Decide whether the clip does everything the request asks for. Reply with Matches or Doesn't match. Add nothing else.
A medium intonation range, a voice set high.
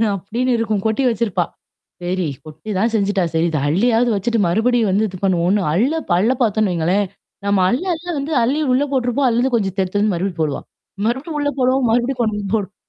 Matches